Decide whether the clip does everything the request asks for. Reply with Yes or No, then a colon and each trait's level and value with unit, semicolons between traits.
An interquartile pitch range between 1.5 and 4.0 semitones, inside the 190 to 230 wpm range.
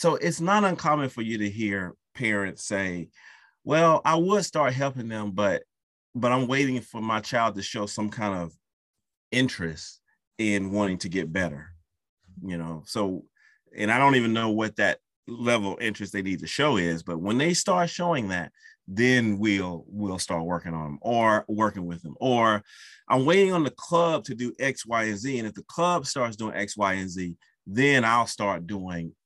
No: average, 5.1 semitones; average, 195 wpm